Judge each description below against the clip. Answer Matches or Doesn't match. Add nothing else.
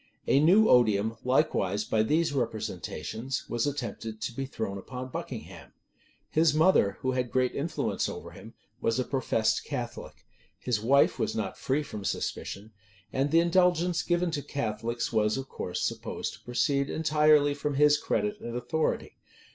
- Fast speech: Doesn't match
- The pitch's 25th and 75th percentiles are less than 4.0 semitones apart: Doesn't match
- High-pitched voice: Doesn't match